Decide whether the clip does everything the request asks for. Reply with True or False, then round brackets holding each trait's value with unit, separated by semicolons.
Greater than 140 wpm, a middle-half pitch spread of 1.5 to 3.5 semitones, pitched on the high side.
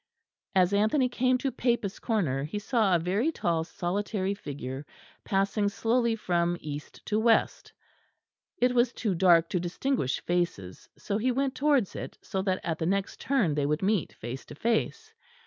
False (165 wpm; 5.6 semitones; 200 Hz)